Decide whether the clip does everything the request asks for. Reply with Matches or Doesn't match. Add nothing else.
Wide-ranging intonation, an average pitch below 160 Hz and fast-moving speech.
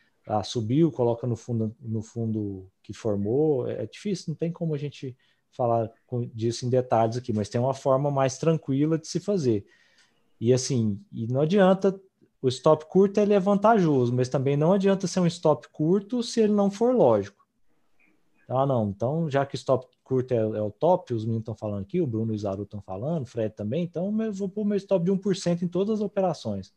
Matches